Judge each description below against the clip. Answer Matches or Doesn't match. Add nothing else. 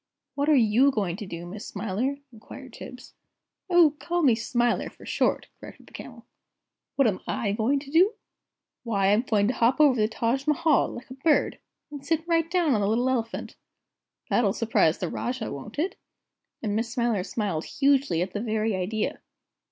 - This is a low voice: Doesn't match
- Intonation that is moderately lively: Matches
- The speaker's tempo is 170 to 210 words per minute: Matches